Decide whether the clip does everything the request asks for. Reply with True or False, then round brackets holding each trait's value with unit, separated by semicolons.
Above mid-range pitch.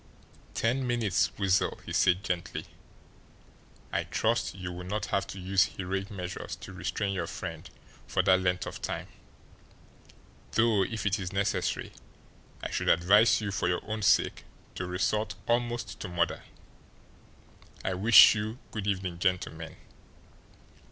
False (95 Hz)